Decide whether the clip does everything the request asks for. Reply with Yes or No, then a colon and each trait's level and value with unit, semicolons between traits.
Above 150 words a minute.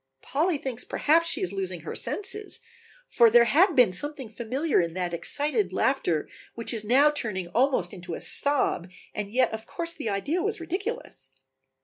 Yes: average, 170 wpm